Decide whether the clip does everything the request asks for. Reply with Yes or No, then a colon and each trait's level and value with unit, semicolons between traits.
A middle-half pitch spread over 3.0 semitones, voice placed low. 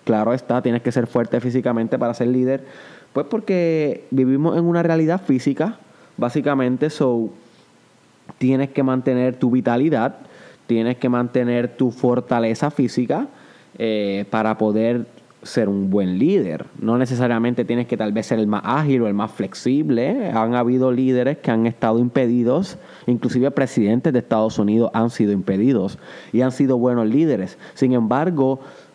No: narrow, 2.6 semitones; low, 125 Hz